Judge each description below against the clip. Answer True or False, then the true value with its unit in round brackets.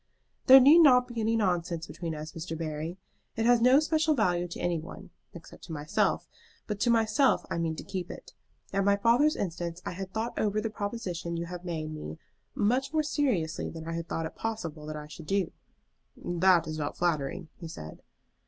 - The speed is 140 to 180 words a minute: False (200 wpm)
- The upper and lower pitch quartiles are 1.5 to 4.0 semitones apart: False (5.6 semitones)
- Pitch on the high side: False (180 Hz)